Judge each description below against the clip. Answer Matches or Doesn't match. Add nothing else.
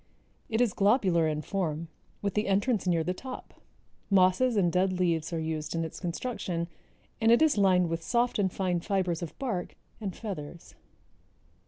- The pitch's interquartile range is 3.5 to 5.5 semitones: Matches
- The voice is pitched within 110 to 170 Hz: Doesn't match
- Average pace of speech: Matches